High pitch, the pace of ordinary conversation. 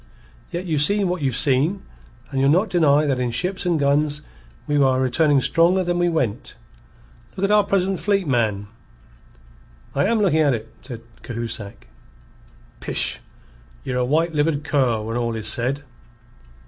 No: medium, 145 Hz; average, 160 wpm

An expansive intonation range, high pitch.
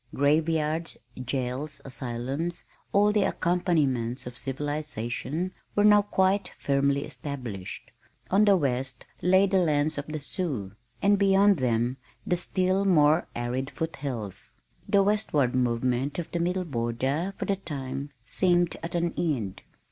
No: wide, 5.9 semitones; medium, 150 Hz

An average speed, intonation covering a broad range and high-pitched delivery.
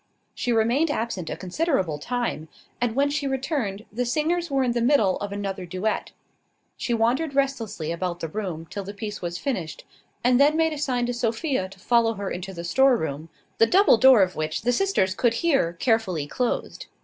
Yes: average, 190 wpm; wide, 6.2 semitones; high, 230 Hz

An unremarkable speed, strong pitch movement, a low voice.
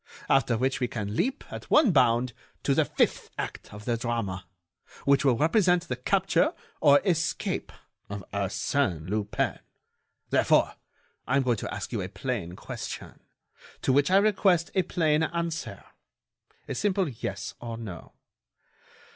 Yes: average, 145 wpm; wide, 7.4 semitones; low, 130 Hz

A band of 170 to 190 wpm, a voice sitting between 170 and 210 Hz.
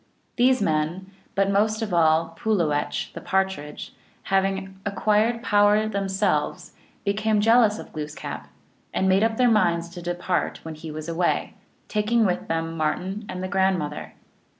No: average, 150 wpm; high, 190 Hz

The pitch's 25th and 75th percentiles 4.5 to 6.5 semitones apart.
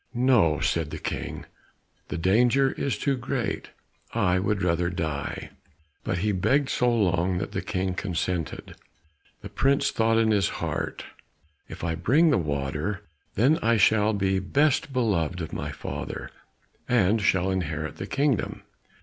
Yes: average, 5.2 semitones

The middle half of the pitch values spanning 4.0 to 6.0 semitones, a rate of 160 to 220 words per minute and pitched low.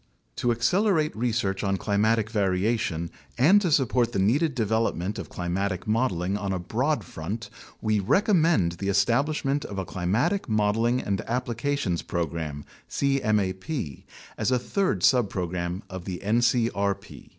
No: average, 5.1 semitones; average, 140 wpm; low, 110 Hz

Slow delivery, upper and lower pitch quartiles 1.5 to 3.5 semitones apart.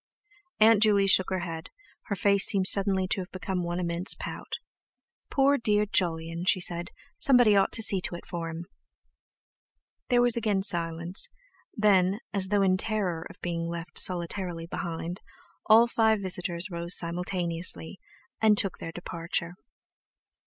No: average, 150 wpm; average, 3.2 semitones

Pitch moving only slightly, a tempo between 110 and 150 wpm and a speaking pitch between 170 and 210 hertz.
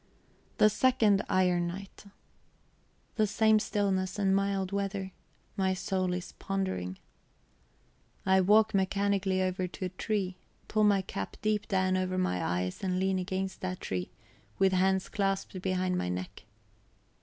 Yes: narrow, 1.4 semitones; average, 140 wpm; high, 190 Hz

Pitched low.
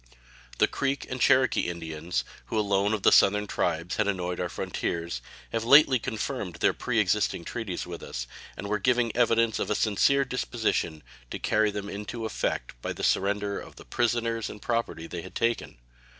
Yes: low, 105 Hz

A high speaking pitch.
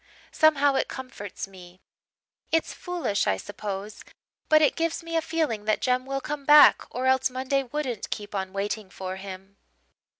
Yes: very high, 255 Hz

